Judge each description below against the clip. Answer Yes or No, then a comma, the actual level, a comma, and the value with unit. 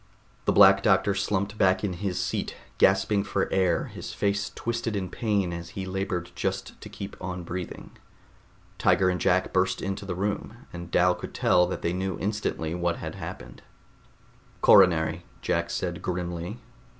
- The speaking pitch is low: Yes, very low, 95 Hz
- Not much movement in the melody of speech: Yes, narrow, 2.2 semitones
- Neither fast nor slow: Yes, average, 160 wpm